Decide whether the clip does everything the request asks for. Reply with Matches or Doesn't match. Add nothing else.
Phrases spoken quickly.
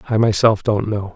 Matches